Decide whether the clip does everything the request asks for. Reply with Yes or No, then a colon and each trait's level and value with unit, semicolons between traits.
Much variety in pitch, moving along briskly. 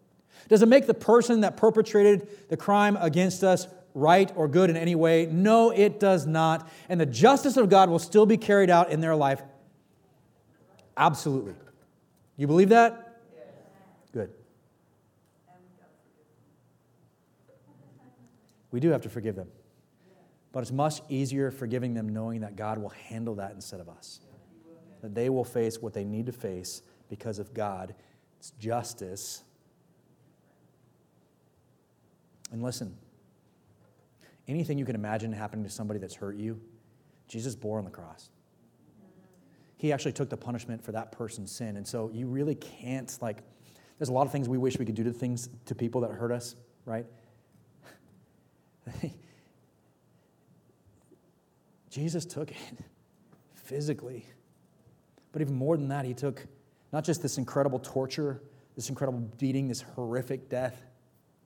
No: wide, 6.2 semitones; average, 145 wpm